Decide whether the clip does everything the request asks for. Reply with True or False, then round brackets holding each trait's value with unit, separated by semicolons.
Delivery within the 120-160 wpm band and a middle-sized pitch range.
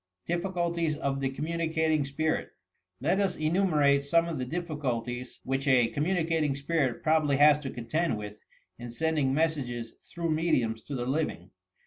True (145 wpm; 3.8 semitones)